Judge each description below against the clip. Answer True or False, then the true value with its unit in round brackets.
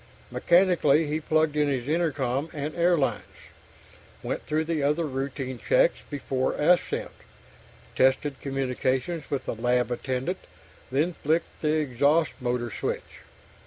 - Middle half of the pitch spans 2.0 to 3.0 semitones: False (3.4 semitones)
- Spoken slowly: True (125 wpm)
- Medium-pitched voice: True (145 Hz)